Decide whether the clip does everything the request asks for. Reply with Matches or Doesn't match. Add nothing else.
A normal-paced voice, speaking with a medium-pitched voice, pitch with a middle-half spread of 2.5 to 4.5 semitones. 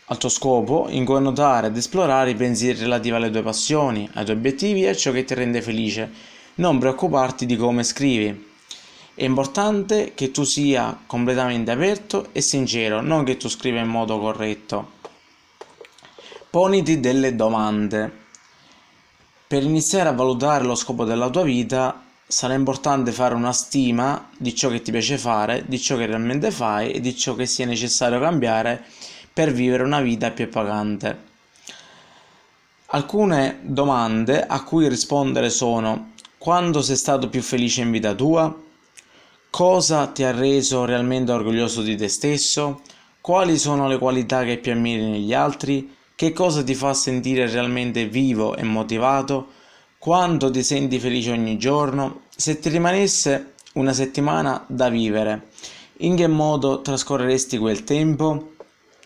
Doesn't match